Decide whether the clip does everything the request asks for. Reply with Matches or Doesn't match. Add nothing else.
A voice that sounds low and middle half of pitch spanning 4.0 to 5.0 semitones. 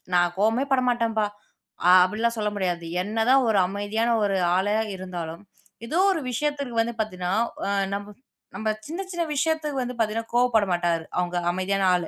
Doesn't match